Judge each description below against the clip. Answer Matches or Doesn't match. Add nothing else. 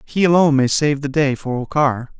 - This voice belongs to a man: Matches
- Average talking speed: Doesn't match